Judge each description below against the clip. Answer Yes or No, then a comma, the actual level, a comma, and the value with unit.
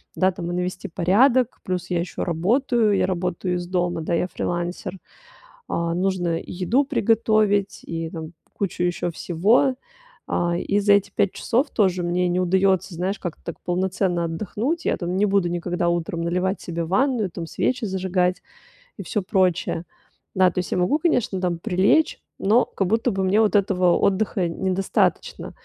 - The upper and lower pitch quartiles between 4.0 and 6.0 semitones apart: No, narrow, 2.6 semitones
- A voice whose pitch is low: No, medium, 185 Hz